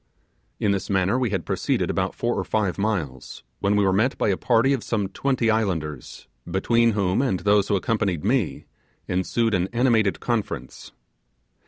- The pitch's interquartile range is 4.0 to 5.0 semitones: No, average, 3.6 semitones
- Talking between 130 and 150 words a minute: No, average, 170 wpm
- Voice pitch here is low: Yes, low, 105 Hz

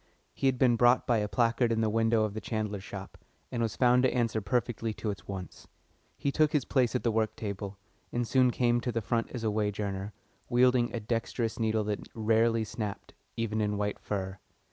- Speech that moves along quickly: Yes, fast, 210 wpm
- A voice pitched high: No, low, 115 Hz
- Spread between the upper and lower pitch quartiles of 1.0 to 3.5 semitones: Yes, narrow, 2.5 semitones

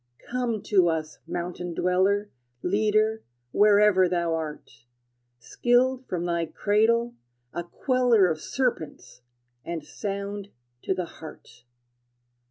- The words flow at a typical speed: No, slow, 105 wpm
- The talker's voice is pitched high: Yes, high, 195 Hz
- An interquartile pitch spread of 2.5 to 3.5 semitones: No, average, 4.1 semitones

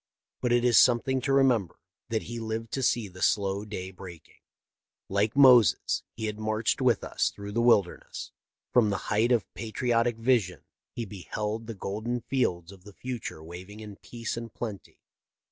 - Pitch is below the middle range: Yes, low, 110 Hz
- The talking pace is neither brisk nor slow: Yes, average, 170 wpm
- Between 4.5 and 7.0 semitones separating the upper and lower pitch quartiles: No, average, 3.1 semitones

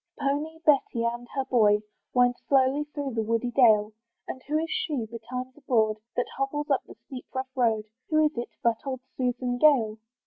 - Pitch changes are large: No, average, 3.4 semitones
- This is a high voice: Yes, very high, 255 Hz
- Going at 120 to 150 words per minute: No, average, 195 wpm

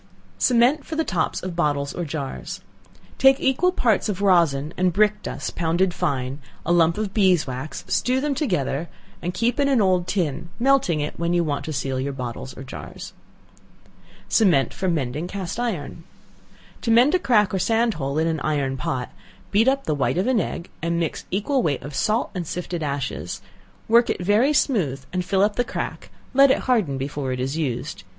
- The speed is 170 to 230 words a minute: Yes, average, 190 wpm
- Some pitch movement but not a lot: No, wide, 7.6 semitones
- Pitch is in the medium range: Yes, medium, 175 Hz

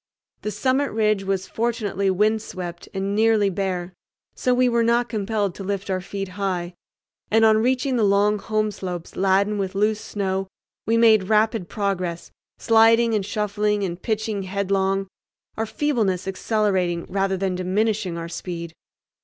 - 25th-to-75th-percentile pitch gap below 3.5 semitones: Yes, narrow, 2.5 semitones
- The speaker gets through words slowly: No, average, 155 wpm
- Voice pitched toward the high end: Yes, high, 200 Hz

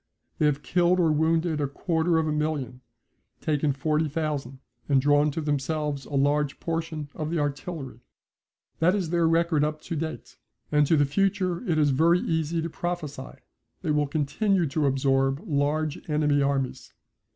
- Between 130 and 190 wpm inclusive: Yes, average, 160 wpm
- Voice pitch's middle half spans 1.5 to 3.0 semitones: Yes, narrow, 2.4 semitones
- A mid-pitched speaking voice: Yes, medium, 150 Hz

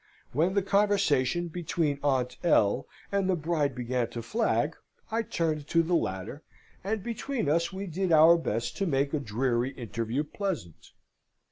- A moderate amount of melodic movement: No, wide, 6.5 semitones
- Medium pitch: Yes, medium, 155 Hz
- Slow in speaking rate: No, average, 155 wpm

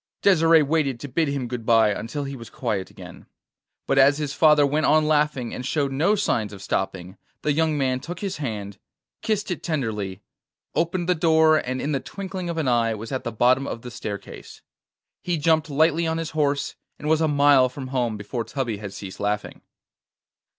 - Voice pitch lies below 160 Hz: Yes, medium, 140 Hz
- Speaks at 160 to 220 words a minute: Yes, average, 200 wpm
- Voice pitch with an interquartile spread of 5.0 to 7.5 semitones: Yes, average, 5.3 semitones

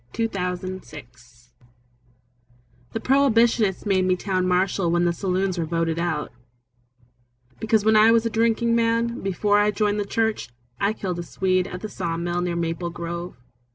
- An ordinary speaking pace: Yes, average, 165 wpm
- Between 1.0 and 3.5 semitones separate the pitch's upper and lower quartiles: No, average, 3.9 semitones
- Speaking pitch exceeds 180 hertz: Yes, high, 190 Hz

